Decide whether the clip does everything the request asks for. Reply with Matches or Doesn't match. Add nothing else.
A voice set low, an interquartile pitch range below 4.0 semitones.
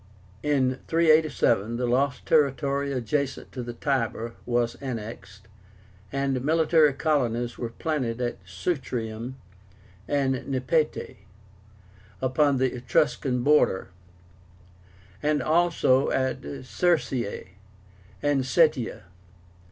Matches